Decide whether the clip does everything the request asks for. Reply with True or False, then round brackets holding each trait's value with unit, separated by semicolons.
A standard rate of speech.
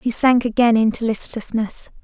True (150 wpm)